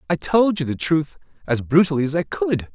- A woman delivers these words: No, male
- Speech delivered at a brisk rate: Yes, fast, 220 wpm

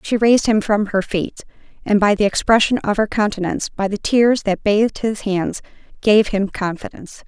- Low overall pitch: No, high, 210 Hz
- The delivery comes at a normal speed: Yes, average, 190 wpm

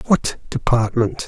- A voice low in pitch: Yes, low, 125 Hz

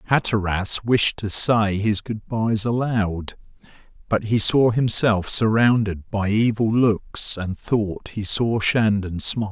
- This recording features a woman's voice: No, male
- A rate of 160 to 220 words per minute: No, average, 145 wpm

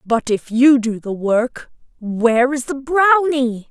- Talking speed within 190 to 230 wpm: No, average, 160 wpm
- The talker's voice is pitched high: Yes, very high, 250 Hz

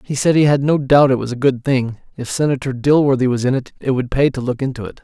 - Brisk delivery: Yes, fast, 285 wpm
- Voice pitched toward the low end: Yes, low, 130 Hz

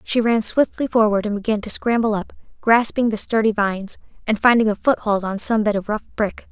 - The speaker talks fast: Yes, fast, 210 wpm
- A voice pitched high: Yes, high, 215 Hz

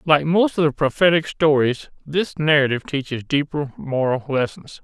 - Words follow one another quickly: No, average, 150 wpm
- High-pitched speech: No, medium, 145 Hz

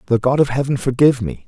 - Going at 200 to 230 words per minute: No, fast, 245 wpm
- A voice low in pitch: Yes, low, 125 Hz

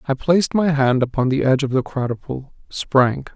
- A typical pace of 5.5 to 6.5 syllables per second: No, 5.3 syllables/s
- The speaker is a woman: No, male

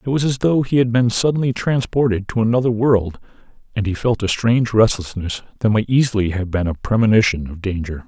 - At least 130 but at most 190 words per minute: No, average, 200 wpm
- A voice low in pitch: Yes, low, 110 Hz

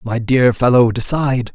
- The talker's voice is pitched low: Yes, low, 125 Hz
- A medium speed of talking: Yes, average, 155 wpm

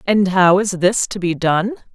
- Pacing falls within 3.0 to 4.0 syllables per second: No, 4.3 syllables/s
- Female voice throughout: Yes, female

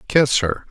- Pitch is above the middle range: No, low, 125 Hz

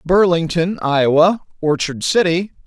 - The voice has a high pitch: No, medium, 165 Hz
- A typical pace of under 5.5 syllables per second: Yes, 4.5 syllables/s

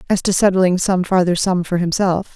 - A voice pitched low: No, medium, 185 Hz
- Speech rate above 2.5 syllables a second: Yes, 5.1 syllables/s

